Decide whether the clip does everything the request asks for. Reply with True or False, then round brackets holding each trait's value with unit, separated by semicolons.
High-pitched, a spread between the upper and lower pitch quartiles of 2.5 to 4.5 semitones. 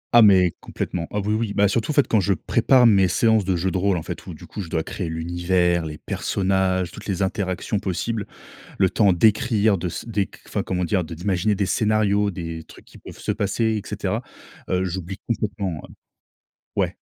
False (95 Hz; 2.9 semitones)